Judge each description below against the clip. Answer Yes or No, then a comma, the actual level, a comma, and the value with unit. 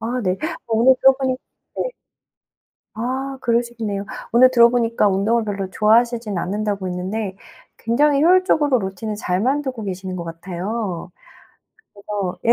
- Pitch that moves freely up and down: No, average, 4.1 semitones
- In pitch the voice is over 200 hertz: Yes, high, 220 Hz